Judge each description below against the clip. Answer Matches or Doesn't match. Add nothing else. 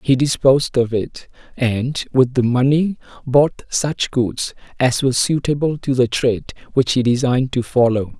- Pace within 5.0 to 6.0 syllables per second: Doesn't match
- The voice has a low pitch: Matches